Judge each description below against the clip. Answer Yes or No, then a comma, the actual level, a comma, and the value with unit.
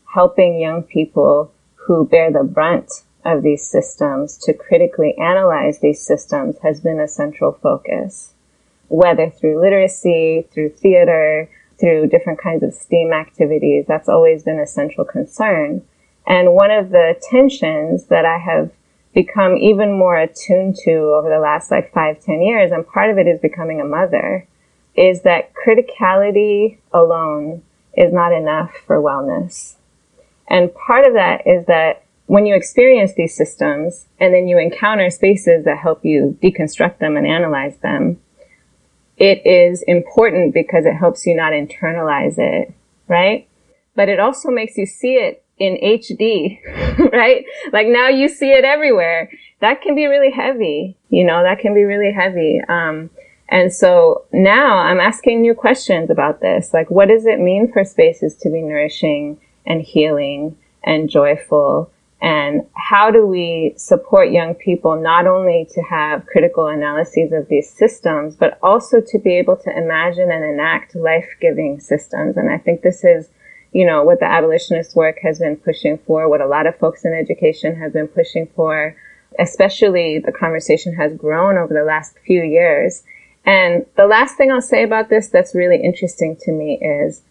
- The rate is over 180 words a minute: No, average, 165 wpm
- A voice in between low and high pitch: Yes, medium, 180 Hz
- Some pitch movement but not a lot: No, wide, 5.9 semitones